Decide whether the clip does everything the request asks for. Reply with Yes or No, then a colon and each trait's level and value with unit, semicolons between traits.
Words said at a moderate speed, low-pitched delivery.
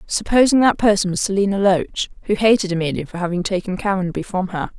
No: average, 190 wpm; high, 195 Hz